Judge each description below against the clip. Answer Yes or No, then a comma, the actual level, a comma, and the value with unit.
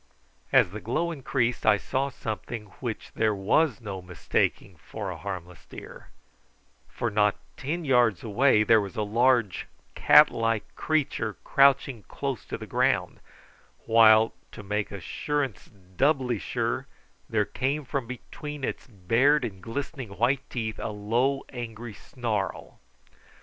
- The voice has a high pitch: No, low, 115 Hz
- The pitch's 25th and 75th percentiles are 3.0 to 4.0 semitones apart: No, average, 4.4 semitones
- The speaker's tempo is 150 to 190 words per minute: No, slow, 135 wpm